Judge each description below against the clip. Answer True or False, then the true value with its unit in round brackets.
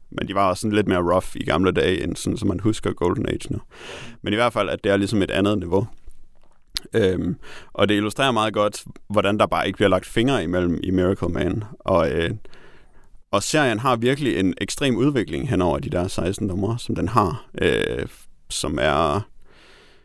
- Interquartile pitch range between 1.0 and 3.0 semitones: True (2.7 semitones)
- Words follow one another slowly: False (200 wpm)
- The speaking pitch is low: True (100 Hz)